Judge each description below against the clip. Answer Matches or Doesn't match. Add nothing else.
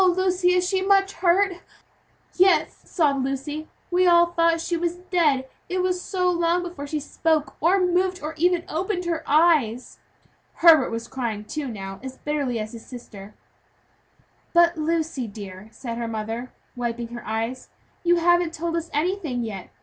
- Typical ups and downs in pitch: Doesn't match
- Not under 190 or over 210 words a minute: Doesn't match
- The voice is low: Doesn't match